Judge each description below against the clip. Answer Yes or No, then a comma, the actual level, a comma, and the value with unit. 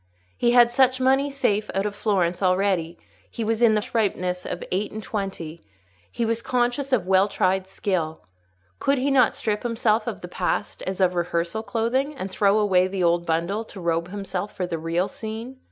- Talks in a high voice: Yes, high, 205 Hz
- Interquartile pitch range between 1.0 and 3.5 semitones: No, average, 4.2 semitones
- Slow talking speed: No, average, 195 wpm